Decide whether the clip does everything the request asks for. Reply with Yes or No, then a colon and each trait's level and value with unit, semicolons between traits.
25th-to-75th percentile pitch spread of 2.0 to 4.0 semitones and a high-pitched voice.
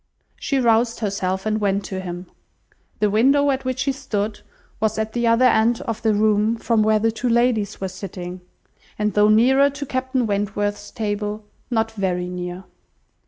Yes: average, 2.7 semitones; high, 215 Hz